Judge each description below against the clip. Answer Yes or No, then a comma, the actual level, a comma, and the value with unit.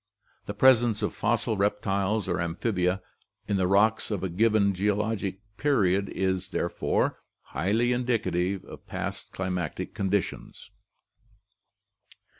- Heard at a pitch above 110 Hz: No, low, 100 Hz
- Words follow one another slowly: Yes, slow, 120 wpm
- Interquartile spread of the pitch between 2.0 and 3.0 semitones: Yes, average, 2.7 semitones